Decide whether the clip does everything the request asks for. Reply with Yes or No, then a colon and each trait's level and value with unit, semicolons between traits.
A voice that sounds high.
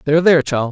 No: medium, 150 Hz